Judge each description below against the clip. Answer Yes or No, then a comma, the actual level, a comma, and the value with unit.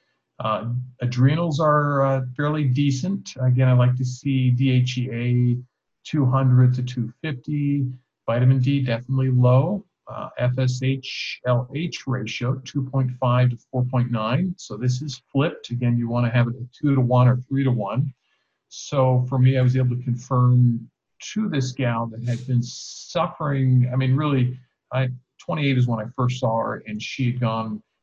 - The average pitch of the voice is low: Yes, low, 130 Hz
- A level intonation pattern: Yes, narrow, 1.6 semitones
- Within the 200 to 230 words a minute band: No, average, 160 wpm